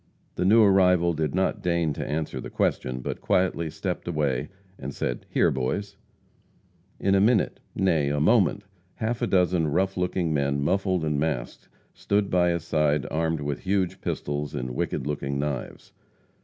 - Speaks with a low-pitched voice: Yes, very low, 80 Hz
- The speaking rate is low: No, average, 165 wpm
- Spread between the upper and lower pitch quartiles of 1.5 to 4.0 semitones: No, average, 4.4 semitones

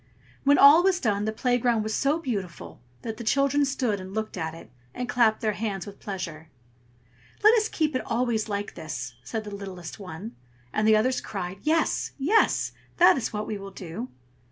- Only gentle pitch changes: No, average, 5.0 semitones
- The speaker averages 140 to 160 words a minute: No, average, 190 wpm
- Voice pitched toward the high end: Yes, high, 220 Hz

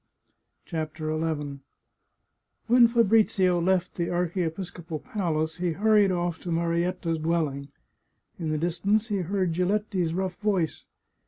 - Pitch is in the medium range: Yes, medium, 175 Hz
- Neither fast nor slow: No, slow, 115 wpm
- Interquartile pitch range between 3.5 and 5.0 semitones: No, average, 3.1 semitones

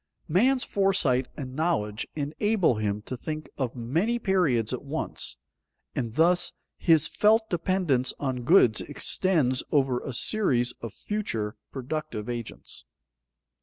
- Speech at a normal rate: No, slow, 125 wpm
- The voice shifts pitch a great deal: Yes, wide, 6.7 semitones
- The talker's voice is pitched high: No, medium, 145 Hz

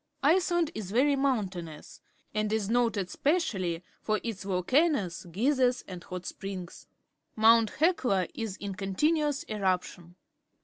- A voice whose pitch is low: No, high, 215 Hz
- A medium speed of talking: No, slow, 125 wpm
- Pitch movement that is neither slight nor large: No, wide, 6.5 semitones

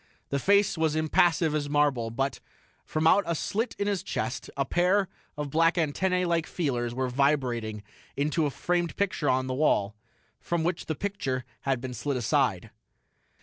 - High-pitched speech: No, medium, 150 Hz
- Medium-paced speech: Yes, average, 170 wpm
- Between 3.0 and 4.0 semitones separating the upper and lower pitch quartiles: No, average, 4.9 semitones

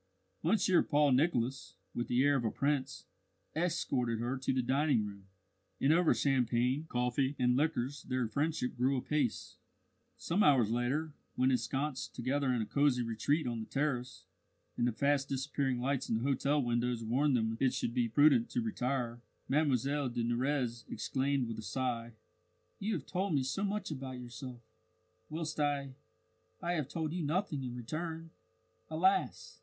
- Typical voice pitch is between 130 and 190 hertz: Yes, low, 135 Hz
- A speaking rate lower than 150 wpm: No, average, 165 wpm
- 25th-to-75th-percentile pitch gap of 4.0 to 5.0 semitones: No, average, 3.4 semitones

